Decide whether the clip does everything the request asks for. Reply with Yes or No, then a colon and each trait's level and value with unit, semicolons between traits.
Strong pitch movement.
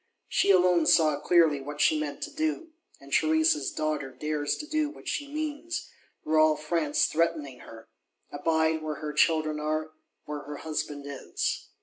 No: average, 3.8 semitones